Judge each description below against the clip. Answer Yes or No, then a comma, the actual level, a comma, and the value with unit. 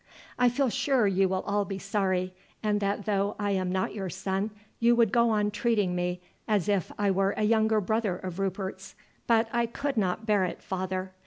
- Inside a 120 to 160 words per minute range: No, average, 200 wpm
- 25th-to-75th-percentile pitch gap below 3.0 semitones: Yes, narrow, 2.6 semitones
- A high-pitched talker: Yes, high, 200 Hz